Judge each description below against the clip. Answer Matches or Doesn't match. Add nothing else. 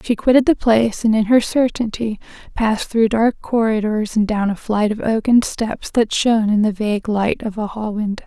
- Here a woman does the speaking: Matches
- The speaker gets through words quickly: Matches